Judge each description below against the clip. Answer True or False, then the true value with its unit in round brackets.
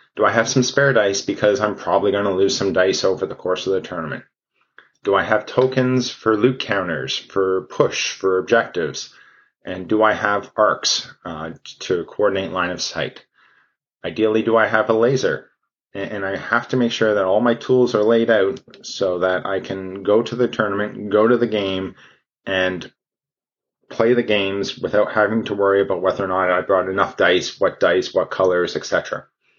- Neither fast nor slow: True (190 wpm)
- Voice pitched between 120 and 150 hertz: False (105 Hz)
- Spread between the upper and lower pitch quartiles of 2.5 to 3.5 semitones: True (3.2 semitones)